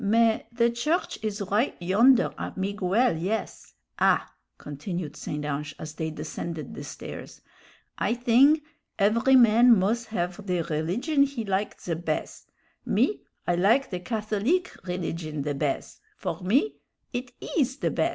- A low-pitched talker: No, high, 205 Hz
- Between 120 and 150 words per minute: Yes, average, 145 wpm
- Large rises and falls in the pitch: Yes, wide, 5.8 semitones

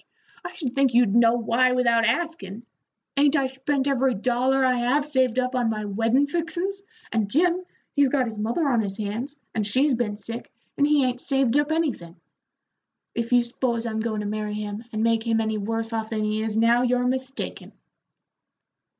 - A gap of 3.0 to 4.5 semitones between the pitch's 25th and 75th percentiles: Yes, average, 3.4 semitones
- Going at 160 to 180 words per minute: No, average, 190 wpm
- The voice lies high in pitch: Yes, high, 240 Hz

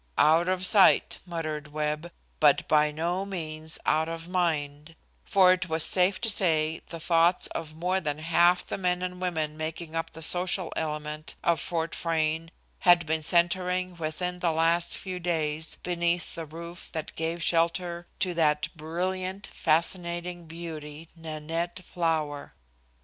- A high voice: No, medium, 165 Hz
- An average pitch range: No, narrow, 2.2 semitones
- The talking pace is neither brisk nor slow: Yes, average, 150 wpm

